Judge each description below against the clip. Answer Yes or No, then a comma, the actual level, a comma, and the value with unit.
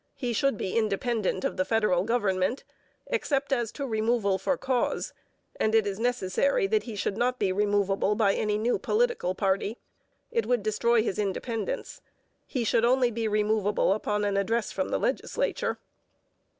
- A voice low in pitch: No, high, 220 Hz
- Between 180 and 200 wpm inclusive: No, average, 165 wpm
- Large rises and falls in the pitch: No, average, 3.5 semitones